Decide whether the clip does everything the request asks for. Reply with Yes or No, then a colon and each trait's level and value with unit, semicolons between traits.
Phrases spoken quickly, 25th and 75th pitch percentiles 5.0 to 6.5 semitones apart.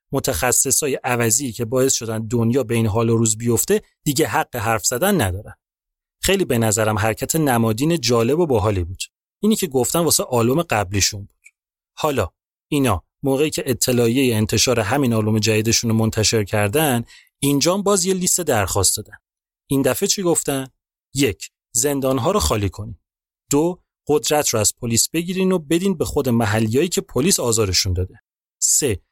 Yes: fast, 160 wpm; average, 5.3 semitones